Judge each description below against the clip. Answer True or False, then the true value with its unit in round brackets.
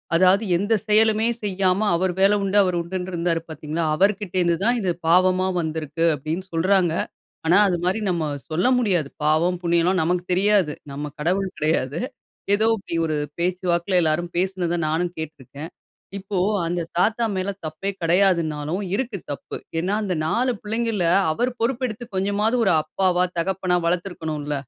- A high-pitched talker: False (180 Hz)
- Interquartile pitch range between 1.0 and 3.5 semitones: True (3.0 semitones)